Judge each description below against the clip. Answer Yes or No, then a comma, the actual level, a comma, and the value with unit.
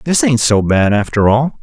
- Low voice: Yes, low, 115 Hz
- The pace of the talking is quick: Yes, fast, 220 wpm